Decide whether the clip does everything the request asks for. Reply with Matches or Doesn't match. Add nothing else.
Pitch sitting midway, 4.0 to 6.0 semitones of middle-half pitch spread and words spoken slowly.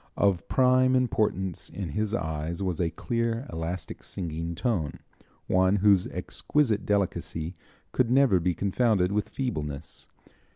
Doesn't match